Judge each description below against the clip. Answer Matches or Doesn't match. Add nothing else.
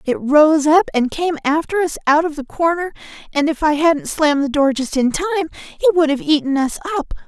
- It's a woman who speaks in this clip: Matches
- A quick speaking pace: Matches